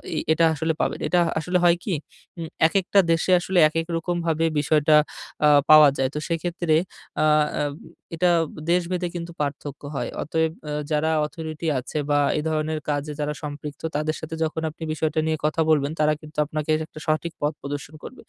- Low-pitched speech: No, medium, 155 Hz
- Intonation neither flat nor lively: No, narrow, 1.7 semitones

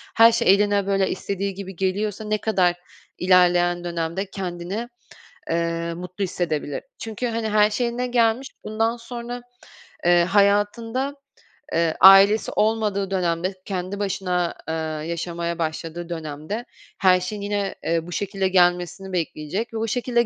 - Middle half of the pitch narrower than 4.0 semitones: Yes, average, 3.5 semitones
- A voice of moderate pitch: No, high, 195 Hz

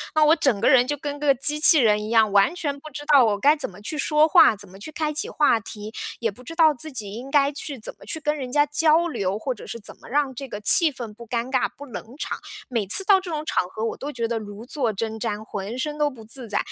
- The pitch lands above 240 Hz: Yes, very high, 260 Hz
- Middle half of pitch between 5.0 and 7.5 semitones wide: Yes, average, 5.3 semitones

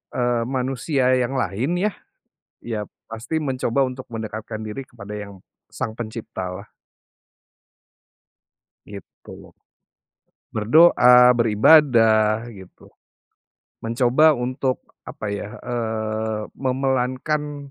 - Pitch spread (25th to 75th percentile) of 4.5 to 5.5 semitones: No, average, 3.4 semitones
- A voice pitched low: Yes, low, 120 Hz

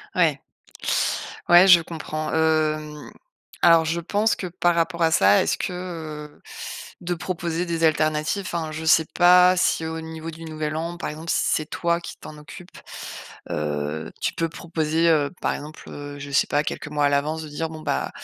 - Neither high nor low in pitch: Yes, medium, 160 Hz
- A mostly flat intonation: Yes, narrow, 1.9 semitones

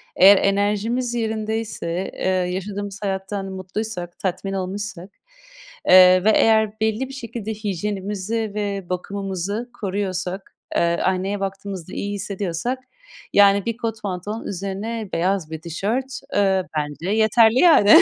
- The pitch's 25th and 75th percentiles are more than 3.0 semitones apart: No, narrow, 2.6 semitones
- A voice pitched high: Yes, high, 200 Hz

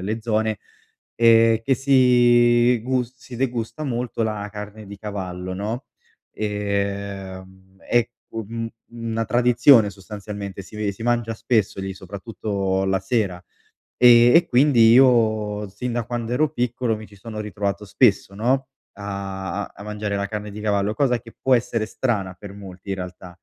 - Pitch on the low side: Yes, low, 110 Hz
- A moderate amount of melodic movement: Yes, average, 3.2 semitones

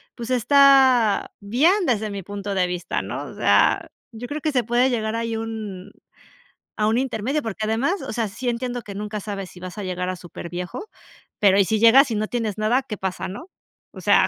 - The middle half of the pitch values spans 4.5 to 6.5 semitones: No, average, 3.8 semitones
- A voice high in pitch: Yes, high, 220 Hz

